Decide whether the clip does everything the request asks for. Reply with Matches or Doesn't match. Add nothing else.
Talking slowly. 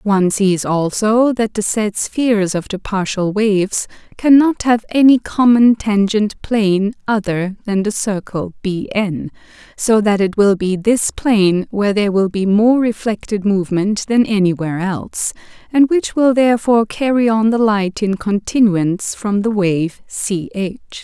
Doesn't match